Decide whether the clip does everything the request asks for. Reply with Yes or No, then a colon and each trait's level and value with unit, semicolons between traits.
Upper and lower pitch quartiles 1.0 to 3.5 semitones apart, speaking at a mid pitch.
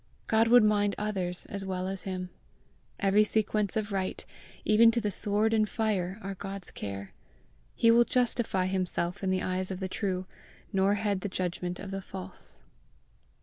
No: narrow, 2.4 semitones; high, 195 Hz